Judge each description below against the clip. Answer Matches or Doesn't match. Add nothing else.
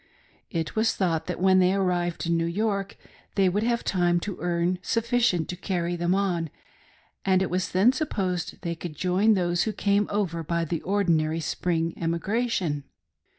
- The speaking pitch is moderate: Matches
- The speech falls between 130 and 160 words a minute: Doesn't match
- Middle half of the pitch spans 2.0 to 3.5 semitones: Matches